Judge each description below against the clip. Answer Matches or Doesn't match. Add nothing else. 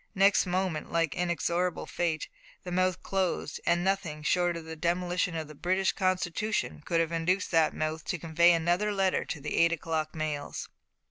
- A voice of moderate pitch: Matches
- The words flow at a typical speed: Matches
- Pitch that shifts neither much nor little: Doesn't match